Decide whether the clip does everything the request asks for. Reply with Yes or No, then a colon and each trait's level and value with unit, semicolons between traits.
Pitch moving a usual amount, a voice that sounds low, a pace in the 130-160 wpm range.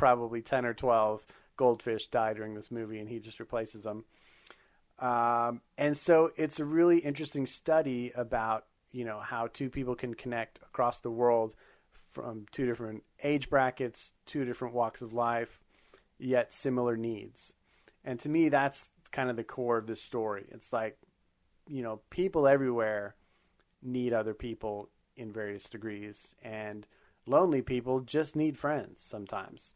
Yes: average, 3.1 semitones; low, 120 Hz; average, 155 wpm